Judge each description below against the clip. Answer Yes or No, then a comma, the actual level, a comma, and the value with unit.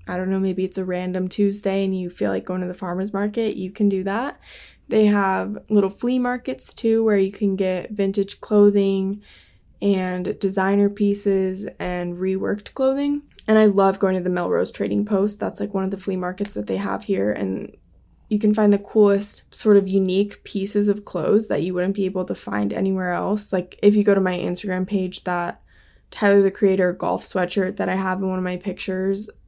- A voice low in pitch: No, high, 195 Hz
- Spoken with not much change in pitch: Yes, narrow, 1.8 semitones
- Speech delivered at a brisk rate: Yes, fast, 210 wpm